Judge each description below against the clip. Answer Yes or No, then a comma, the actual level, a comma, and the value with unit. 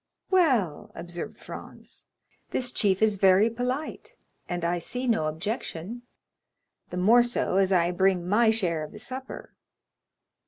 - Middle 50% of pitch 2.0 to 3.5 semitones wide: No, wide, 5.5 semitones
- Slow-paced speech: Yes, slow, 130 wpm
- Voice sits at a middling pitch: No, high, 200 Hz